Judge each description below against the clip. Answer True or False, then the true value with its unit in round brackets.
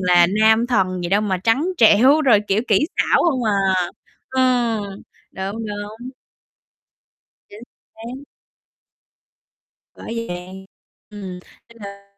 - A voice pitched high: True (210 Hz)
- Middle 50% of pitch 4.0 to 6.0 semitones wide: False (3.5 semitones)